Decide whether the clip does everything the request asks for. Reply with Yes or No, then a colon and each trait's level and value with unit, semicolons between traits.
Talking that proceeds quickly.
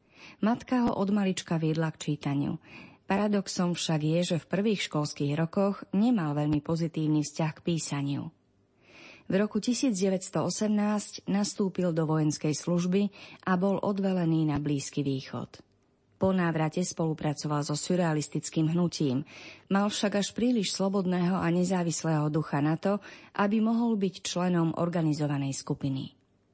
No: average, 125 wpm